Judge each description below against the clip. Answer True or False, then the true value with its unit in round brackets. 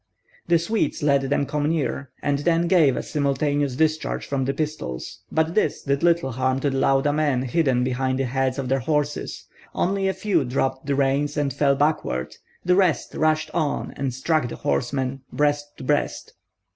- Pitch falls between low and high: True (145 Hz)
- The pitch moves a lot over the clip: False (2.7 semitones)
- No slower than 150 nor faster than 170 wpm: False (185 wpm)